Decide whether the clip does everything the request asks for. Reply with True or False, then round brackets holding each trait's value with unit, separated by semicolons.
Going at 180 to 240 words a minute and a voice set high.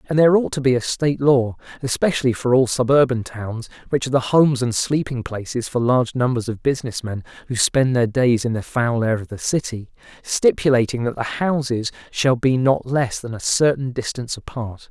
False (200 wpm; 125 Hz)